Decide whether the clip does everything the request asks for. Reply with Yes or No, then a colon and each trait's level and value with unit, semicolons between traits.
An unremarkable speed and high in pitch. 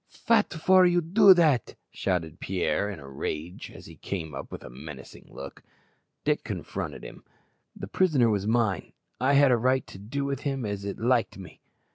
No: average, 185 wpm; low, 115 Hz